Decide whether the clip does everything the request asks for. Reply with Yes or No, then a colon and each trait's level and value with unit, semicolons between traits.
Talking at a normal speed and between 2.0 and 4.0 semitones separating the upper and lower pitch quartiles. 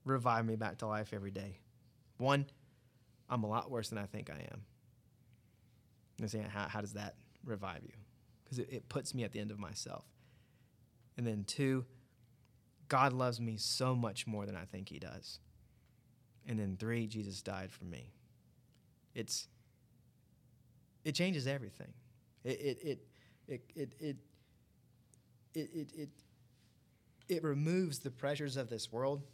Yes: average, 155 wpm; average, 2.7 semitones